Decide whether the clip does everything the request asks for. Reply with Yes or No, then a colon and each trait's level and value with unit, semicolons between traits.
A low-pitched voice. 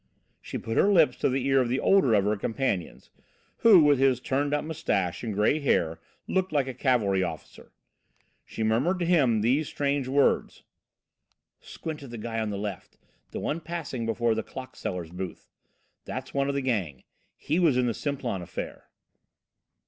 Yes: low, 130 Hz